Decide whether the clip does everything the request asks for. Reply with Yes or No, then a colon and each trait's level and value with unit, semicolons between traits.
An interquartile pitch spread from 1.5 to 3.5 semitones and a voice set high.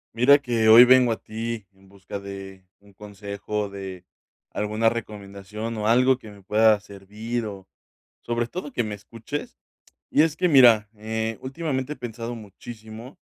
No: average, 2.9 semitones; low, 110 Hz